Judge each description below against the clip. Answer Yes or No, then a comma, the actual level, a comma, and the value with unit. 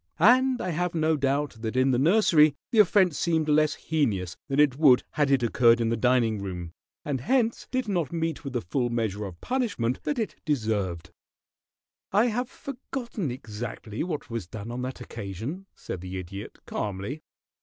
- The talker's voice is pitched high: No, low, 135 Hz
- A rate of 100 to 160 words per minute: No, average, 175 wpm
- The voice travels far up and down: Yes, wide, 7.4 semitones